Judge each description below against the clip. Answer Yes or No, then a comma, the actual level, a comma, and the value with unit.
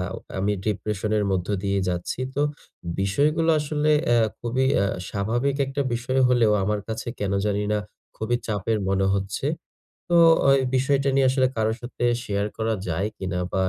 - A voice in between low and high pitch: No, low, 110 Hz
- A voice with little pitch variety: No, average, 4.7 semitones